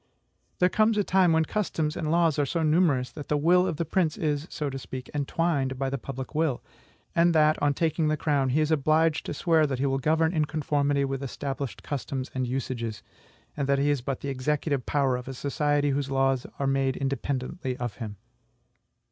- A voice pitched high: No, medium, 145 Hz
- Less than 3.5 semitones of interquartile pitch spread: Yes, average, 2.9 semitones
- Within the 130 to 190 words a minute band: No, fast, 205 wpm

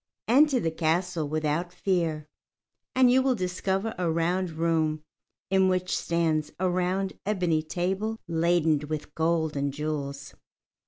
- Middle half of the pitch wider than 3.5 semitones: No, average, 3.2 semitones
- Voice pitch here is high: No, medium, 170 Hz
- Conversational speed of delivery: No, slow, 130 wpm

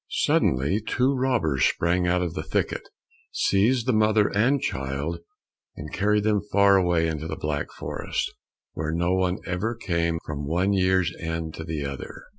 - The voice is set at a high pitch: No, very low, 90 Hz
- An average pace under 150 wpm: No, average, 160 wpm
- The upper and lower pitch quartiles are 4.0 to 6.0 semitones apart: Yes, average, 4.4 semitones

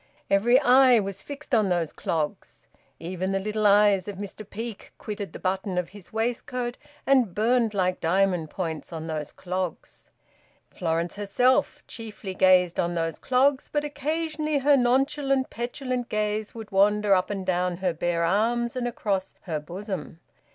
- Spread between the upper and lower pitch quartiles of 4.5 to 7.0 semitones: Yes, average, 5.1 semitones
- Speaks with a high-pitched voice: Yes, high, 205 Hz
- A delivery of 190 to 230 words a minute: No, average, 155 wpm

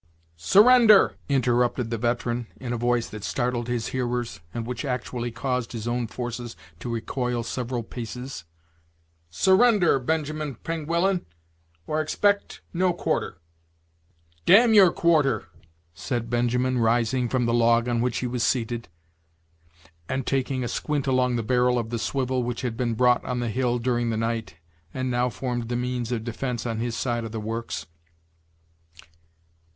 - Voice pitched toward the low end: Yes, low, 125 Hz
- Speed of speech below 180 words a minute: Yes, average, 155 wpm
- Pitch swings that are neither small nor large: No, narrow, 1.9 semitones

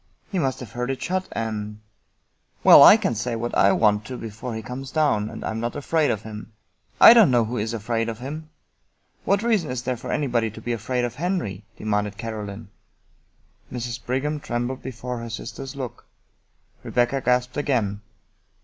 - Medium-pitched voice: No, low, 120 Hz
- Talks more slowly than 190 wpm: No, average, 200 wpm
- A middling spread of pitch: Yes, average, 3.2 semitones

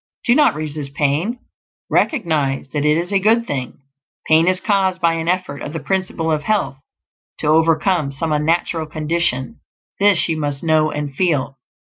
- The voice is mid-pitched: Yes, medium, 160 Hz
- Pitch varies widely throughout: No, average, 3.9 semitones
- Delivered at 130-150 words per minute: No, average, 165 wpm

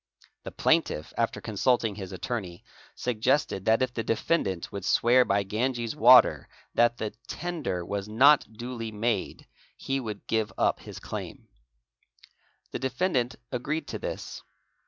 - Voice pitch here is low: Yes, low, 115 Hz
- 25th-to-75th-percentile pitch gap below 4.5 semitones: Yes, average, 3.7 semitones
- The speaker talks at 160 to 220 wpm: No, slow, 135 wpm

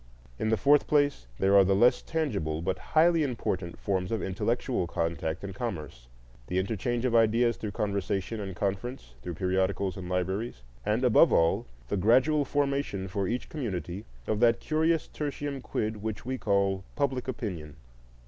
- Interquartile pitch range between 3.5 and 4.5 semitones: No, average, 5.1 semitones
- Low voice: Yes, low, 105 Hz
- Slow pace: No, average, 160 wpm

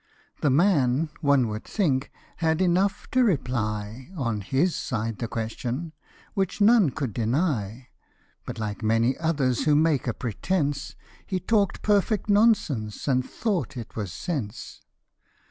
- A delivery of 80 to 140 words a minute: Yes, slow, 135 wpm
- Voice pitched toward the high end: No, medium, 140 Hz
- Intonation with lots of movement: Yes, wide, 7.4 semitones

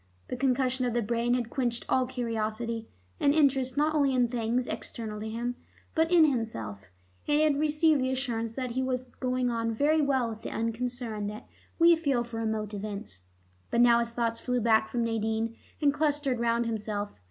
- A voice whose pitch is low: No, high, 240 Hz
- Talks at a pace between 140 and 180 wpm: No, average, 190 wpm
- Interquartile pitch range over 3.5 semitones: No, average, 2.7 semitones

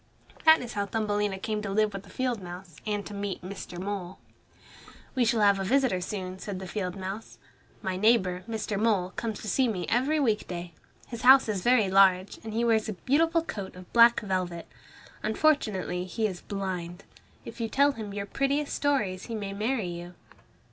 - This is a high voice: Yes, high, 205 Hz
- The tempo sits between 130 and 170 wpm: No, average, 190 wpm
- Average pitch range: Yes, average, 3.7 semitones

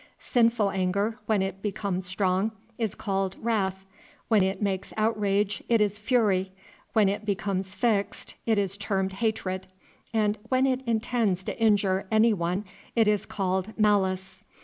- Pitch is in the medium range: No, high, 200 Hz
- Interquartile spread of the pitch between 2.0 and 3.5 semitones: Yes, narrow, 2.4 semitones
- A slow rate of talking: No, average, 150 wpm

